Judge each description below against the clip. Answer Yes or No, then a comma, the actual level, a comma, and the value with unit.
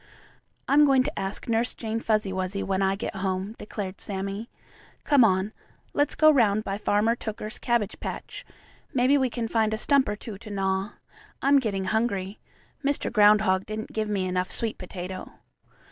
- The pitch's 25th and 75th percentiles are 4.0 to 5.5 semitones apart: No, average, 3.3 semitones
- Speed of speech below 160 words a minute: No, average, 170 wpm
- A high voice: Yes, high, 210 Hz